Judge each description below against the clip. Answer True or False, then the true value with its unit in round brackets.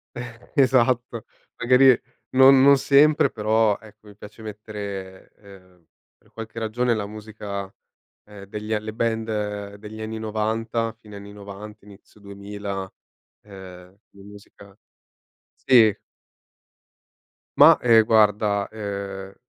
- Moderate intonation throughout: False (2.0 semitones)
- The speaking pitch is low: True (105 Hz)